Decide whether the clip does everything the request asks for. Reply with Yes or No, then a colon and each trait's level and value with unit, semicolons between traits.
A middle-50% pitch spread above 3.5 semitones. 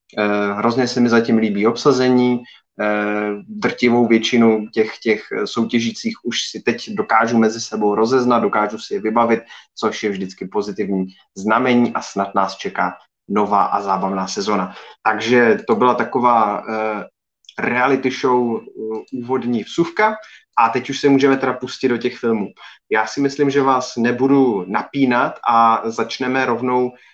No: average, 2.8 semitones